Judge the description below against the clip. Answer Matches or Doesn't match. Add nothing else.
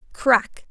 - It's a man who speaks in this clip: Doesn't match